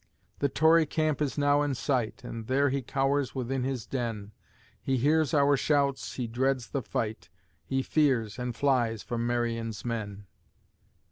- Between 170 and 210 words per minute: No, average, 155 wpm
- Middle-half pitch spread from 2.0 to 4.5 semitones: Yes, average, 3.4 semitones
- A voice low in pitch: Yes, low, 130 Hz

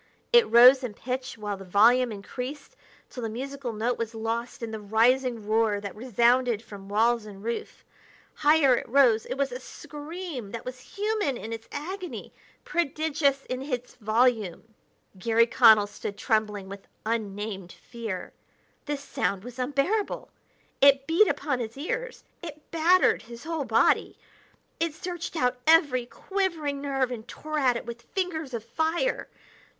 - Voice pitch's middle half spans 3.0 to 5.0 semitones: Yes, average, 4.7 semitones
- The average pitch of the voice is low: No, very high, 250 Hz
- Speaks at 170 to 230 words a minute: No, average, 155 wpm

